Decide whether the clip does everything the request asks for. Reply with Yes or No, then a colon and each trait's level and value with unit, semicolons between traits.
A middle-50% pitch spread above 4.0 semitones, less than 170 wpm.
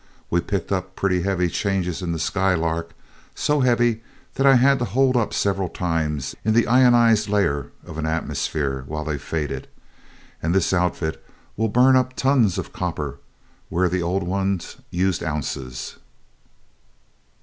Yes: wide, 5.5 semitones; average, 150 wpm